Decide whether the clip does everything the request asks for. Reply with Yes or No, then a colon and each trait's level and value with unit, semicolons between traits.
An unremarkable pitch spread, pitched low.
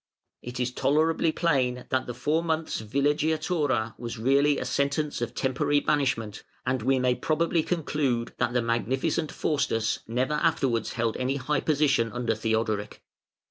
Yes: average, 4.1 semitones; low, 130 Hz